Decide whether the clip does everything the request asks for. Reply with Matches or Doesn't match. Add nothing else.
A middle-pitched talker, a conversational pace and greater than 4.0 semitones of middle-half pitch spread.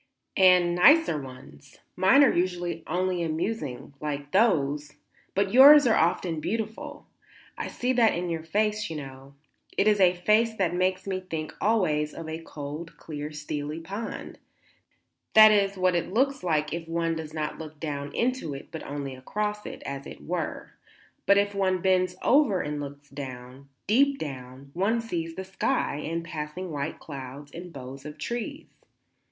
Matches